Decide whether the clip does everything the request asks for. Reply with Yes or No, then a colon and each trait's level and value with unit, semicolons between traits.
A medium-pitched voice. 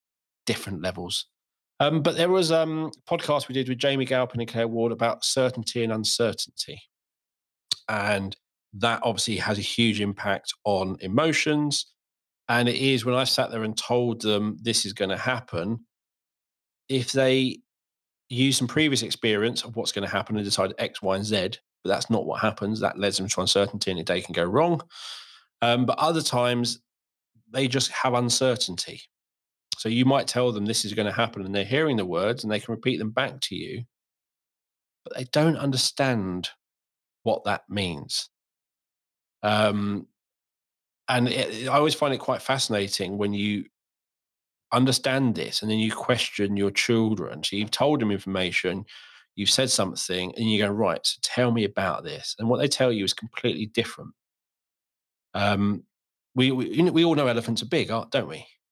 No: low, 115 Hz